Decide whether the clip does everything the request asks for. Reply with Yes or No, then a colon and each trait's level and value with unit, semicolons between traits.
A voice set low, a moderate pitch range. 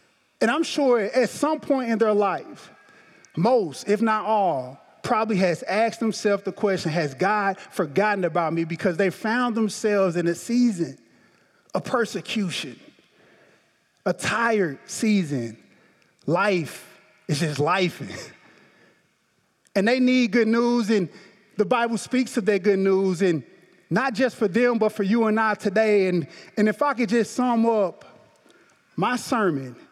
No: high, 210 Hz; average, 4.0 semitones